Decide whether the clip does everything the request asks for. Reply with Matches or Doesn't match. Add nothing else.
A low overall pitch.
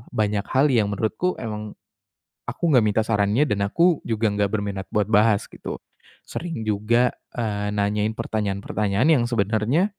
Matches